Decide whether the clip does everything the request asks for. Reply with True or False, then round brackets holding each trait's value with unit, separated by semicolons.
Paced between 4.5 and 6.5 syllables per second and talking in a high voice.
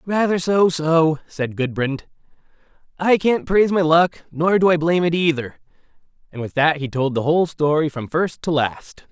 False (4.8 syllables/s; 160 Hz)